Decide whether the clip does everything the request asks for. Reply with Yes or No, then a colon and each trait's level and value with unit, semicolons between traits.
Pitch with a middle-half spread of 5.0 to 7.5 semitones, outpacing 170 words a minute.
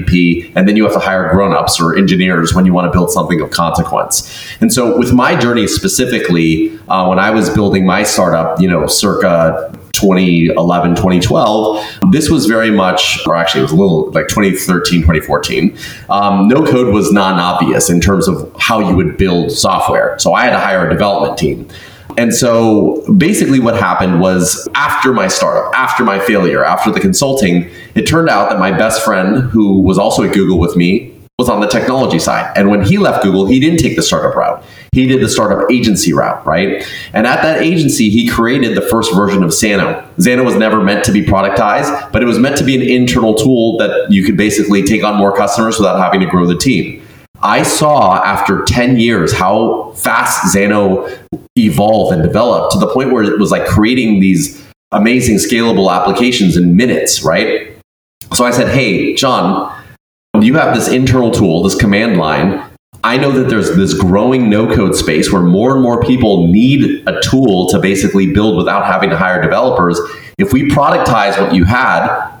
No: average, 4.4 semitones; average, 190 wpm